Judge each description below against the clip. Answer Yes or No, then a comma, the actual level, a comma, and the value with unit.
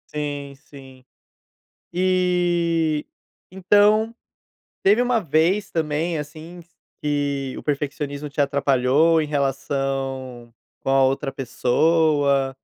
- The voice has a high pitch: No, medium, 150 Hz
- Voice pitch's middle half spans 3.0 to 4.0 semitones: Yes, average, 3.6 semitones